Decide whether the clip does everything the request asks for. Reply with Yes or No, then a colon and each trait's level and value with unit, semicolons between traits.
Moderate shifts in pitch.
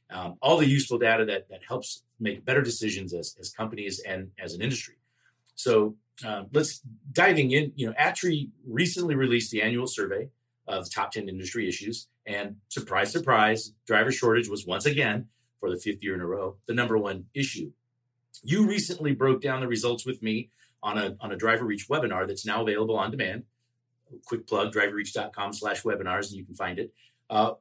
Yes: average, 3.9 semitones